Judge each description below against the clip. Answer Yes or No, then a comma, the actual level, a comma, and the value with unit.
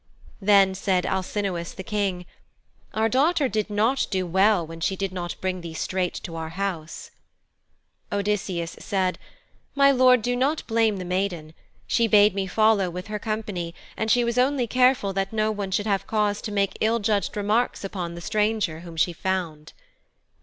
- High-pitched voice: Yes, high, 200 Hz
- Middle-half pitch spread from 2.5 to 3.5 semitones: Yes, average, 3.2 semitones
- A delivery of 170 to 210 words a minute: Yes, average, 175 wpm